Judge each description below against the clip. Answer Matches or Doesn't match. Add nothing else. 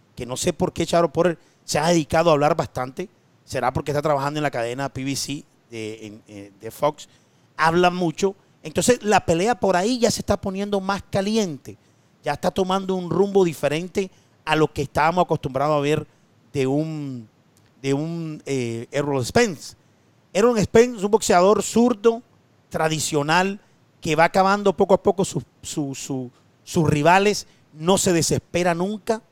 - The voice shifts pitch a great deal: Matches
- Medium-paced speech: Matches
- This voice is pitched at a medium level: Matches